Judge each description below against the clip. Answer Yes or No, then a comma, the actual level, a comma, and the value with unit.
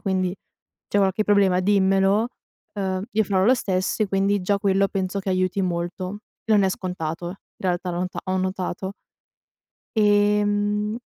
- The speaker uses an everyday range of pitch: No, narrow, 1.8 semitones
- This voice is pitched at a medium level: No, high, 195 Hz